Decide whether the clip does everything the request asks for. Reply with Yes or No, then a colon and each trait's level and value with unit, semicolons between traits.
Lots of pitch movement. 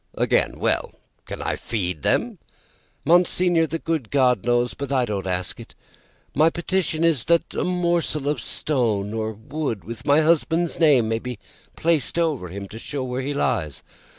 Yes: wide, 6.5 semitones